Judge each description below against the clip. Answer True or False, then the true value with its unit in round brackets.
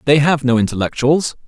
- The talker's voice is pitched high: False (135 Hz)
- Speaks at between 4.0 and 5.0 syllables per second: False (5.6 syllables/s)